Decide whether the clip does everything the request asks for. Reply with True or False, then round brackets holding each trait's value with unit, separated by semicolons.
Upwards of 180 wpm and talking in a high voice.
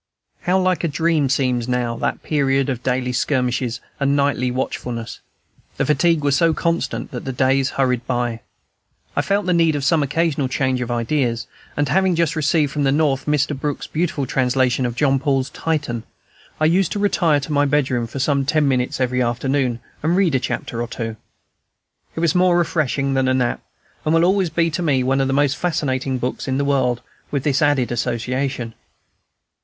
False (190 wpm; 135 Hz)